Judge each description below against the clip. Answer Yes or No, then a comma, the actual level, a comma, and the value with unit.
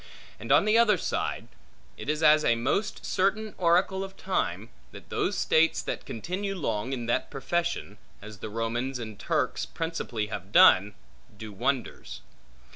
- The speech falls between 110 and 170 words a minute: Yes, average, 150 wpm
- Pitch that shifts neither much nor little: No, wide, 8.4 semitones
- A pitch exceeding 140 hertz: No, low, 135 Hz